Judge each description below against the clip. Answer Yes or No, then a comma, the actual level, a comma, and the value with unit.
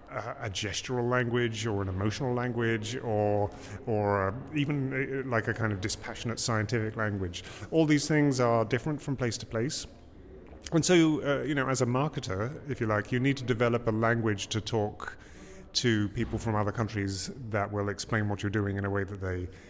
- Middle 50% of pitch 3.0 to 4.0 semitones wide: Yes, average, 3.5 semitones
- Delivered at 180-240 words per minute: Yes, average, 185 wpm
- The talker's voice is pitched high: No, low, 115 Hz